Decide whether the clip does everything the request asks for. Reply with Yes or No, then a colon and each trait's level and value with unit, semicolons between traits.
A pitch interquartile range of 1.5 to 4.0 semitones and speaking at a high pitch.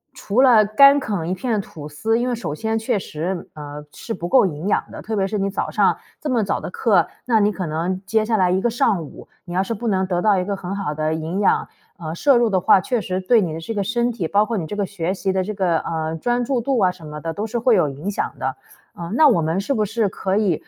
No: average, 4.5 semitones; high, 195 Hz